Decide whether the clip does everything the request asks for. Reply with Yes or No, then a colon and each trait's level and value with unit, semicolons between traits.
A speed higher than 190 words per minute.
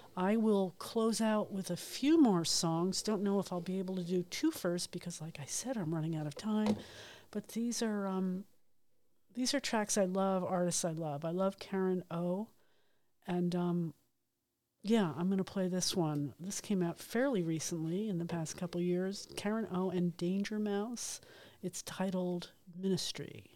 No: average, 185 wpm